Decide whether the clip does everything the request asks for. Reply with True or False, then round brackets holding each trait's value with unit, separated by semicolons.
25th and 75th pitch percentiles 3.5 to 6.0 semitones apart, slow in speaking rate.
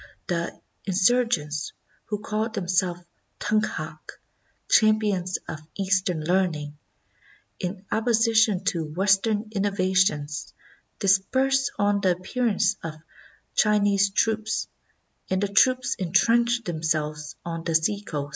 True (4.0 semitones; 105 wpm)